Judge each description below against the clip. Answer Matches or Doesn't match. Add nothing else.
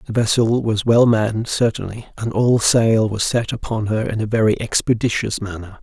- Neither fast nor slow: Matches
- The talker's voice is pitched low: Matches